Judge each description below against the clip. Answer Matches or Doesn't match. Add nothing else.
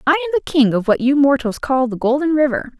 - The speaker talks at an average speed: Doesn't match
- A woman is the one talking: Matches